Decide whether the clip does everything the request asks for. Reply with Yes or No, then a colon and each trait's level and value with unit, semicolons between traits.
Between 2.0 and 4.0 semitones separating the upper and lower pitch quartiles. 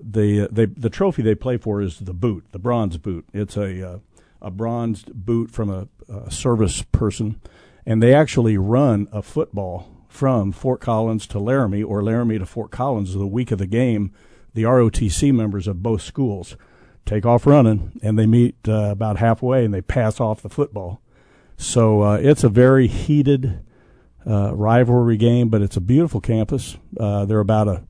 Yes: average, 3.2 semitones